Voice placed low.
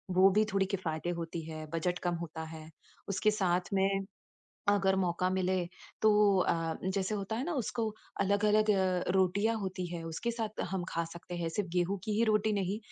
No: high, 190 Hz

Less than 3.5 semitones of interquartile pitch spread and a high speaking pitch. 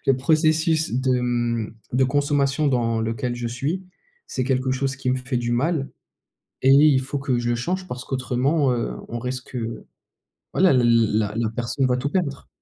No: average, 2.8 semitones; low, 130 Hz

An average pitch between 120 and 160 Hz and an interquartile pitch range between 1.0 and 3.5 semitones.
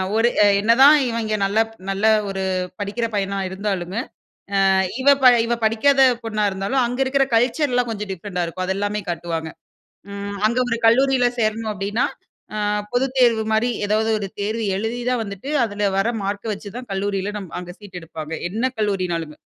No: high, 210 Hz; average, 3.2 semitones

